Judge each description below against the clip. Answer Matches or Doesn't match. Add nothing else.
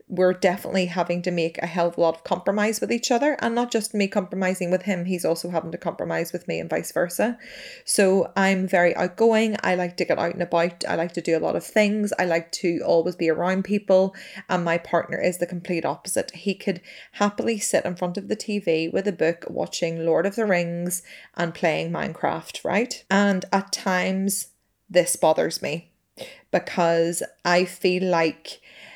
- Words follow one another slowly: Doesn't match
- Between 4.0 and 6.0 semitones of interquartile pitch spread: Doesn't match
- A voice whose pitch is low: Doesn't match